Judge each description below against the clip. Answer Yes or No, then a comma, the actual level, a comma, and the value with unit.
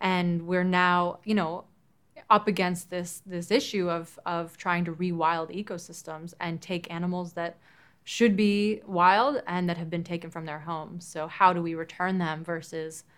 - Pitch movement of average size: No, narrow, 1.5 semitones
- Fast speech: No, average, 175 wpm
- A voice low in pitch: No, medium, 175 Hz